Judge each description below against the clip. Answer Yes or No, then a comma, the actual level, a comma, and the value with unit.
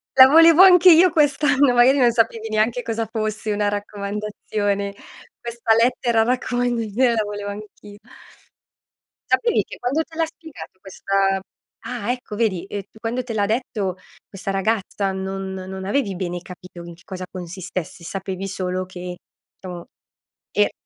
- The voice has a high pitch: Yes, high, 210 Hz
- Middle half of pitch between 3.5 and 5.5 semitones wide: Yes, average, 4.2 semitones